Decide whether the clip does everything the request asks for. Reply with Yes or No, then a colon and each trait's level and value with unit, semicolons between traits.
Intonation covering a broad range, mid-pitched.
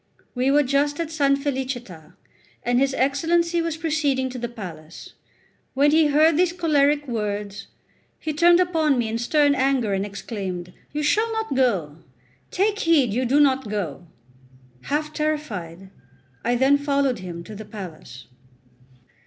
No: wide, 6.4 semitones; very high, 270 Hz